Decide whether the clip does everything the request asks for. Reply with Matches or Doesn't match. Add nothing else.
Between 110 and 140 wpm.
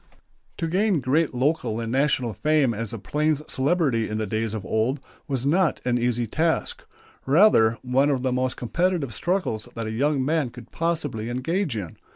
Doesn't match